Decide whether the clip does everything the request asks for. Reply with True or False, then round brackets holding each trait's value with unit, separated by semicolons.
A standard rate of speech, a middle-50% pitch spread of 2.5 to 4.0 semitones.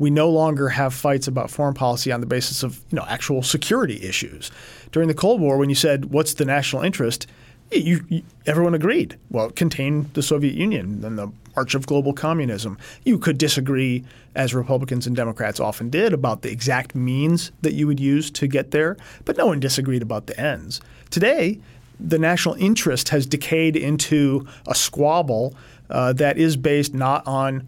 True (185 wpm; 3.5 semitones)